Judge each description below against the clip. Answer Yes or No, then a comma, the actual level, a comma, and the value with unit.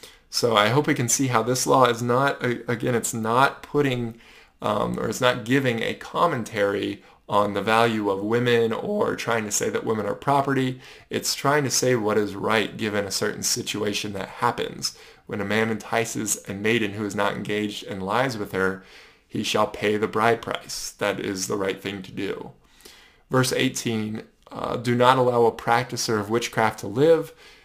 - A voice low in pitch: Yes, low, 115 Hz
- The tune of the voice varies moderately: Yes, average, 3.3 semitones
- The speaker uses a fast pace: No, average, 190 wpm